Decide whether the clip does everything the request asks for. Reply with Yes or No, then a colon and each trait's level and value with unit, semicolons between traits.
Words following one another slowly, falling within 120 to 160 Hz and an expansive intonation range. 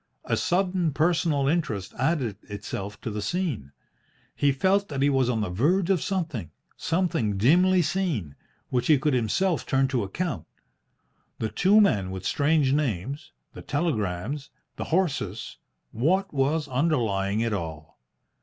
No: average, 145 wpm; medium, 140 Hz; wide, 8.1 semitones